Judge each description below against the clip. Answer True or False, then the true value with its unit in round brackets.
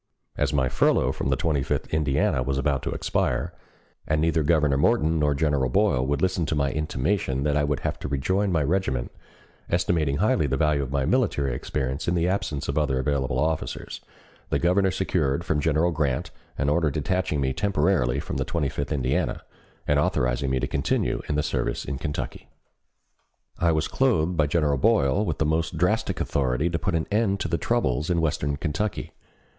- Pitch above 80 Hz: False (75 Hz)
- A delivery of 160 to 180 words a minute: False (190 wpm)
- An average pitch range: True (3.5 semitones)